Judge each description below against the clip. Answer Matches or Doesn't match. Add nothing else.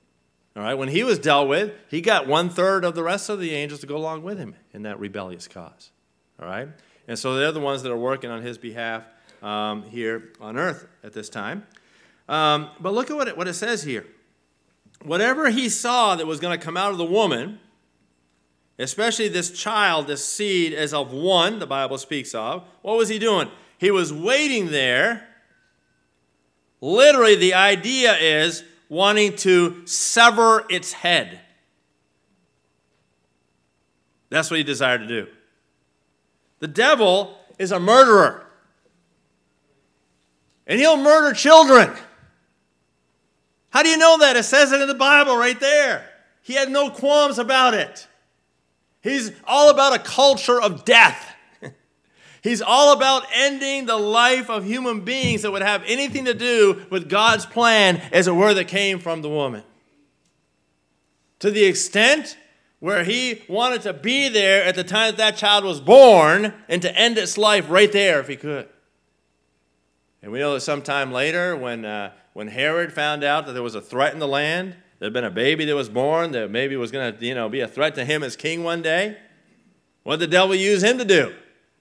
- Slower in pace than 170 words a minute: Doesn't match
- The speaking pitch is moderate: Matches